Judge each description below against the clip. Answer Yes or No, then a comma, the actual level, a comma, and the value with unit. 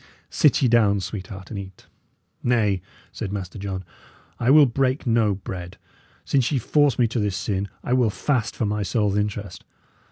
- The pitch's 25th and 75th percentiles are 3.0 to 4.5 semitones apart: Yes, average, 3.8 semitones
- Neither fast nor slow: Yes, average, 170 wpm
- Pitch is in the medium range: No, low, 105 Hz